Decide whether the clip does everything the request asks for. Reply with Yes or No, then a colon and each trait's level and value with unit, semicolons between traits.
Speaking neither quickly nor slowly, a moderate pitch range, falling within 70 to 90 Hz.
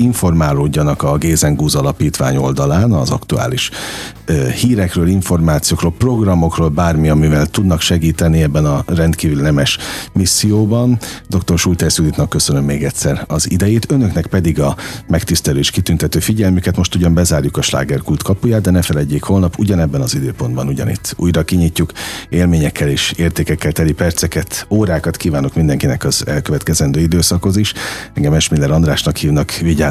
Yes: average, 135 wpm; average, 3.2 semitones; very low, 80 Hz